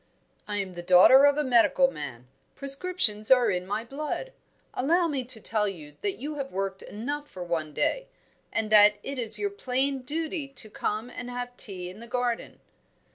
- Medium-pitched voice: No, high, 245 Hz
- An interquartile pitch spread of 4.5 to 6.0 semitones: Yes, average, 5.3 semitones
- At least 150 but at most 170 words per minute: No, average, 185 wpm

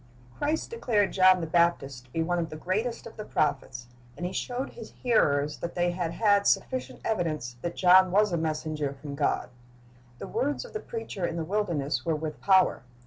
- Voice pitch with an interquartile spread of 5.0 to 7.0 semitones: Yes, average, 5.3 semitones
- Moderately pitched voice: Yes, medium, 175 Hz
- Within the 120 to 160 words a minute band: No, average, 195 wpm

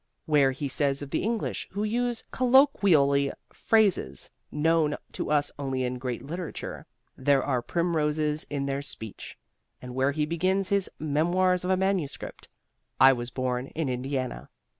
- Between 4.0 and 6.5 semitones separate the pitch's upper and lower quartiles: Yes, average, 5.3 semitones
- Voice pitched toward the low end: No, medium, 150 Hz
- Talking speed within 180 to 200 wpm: No, average, 150 wpm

